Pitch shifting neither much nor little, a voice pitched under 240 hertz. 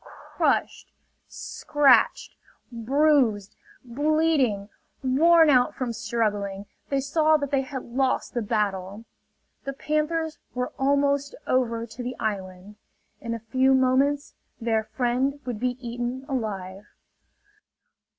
No: average, 4.1 semitones; very high, 255 Hz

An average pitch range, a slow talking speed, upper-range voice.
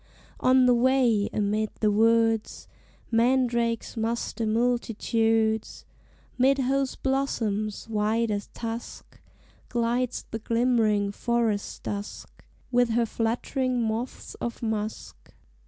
No: narrow, 2.0 semitones; slow, 100 wpm; high, 230 Hz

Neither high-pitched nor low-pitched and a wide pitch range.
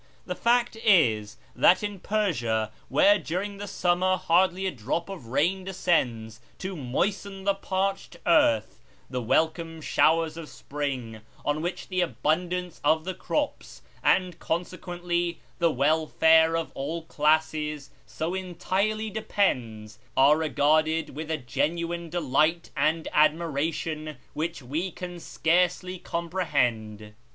No: medium, 165 Hz; average, 3.8 semitones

